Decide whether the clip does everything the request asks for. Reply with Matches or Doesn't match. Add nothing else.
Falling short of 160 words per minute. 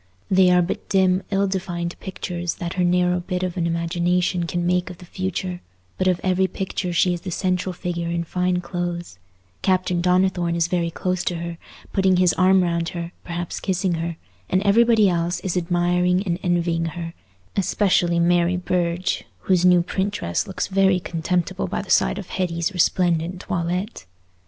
Doesn't match